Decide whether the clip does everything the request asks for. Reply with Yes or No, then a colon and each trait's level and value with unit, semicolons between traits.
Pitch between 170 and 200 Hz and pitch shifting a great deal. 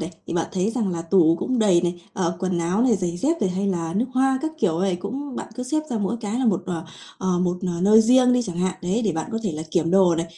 No: high, 190 Hz; average, 4.7 semitones